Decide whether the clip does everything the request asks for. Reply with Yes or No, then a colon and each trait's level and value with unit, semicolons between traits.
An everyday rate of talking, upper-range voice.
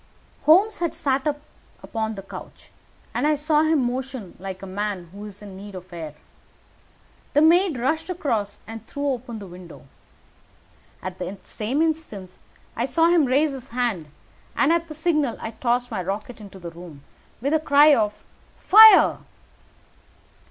Yes: average, 160 wpm; high, 245 Hz